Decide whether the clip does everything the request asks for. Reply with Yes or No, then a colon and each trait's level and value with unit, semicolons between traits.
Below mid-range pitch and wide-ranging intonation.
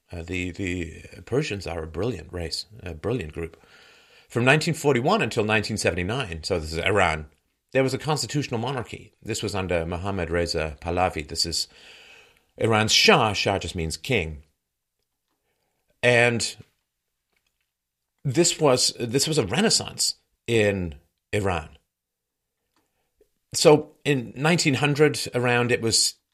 Yes: low, 100 Hz; wide, 6.7 semitones